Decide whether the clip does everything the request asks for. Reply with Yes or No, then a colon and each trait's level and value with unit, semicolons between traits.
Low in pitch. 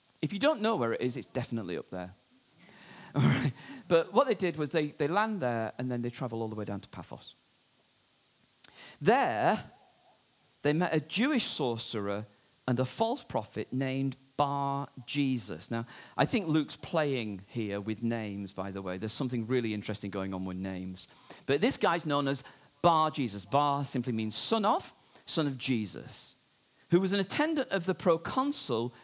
Yes: low, 130 Hz